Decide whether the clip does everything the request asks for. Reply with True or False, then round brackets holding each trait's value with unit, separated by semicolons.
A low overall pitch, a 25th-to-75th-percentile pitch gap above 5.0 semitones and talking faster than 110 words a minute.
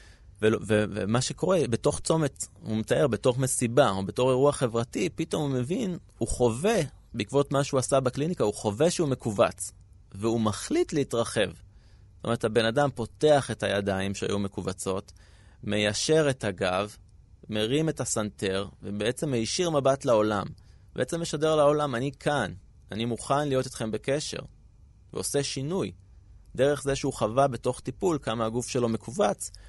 True (120 Hz; 5.4 semitones; 145 wpm)